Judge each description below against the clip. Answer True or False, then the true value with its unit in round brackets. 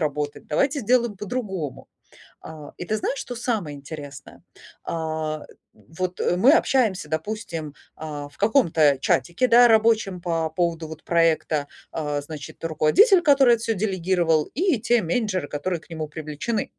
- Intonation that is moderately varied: False (6.4 semitones)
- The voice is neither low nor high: True (170 Hz)